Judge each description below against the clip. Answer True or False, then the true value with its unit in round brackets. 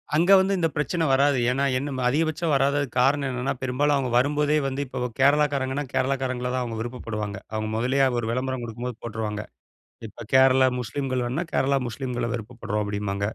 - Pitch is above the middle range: False (130 Hz)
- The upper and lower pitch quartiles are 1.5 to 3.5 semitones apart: True (2.9 semitones)